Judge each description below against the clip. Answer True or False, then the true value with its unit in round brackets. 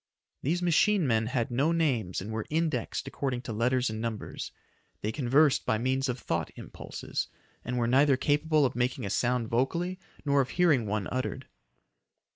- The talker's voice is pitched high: False (130 Hz)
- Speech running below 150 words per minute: False (170 wpm)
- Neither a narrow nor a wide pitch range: True (4.2 semitones)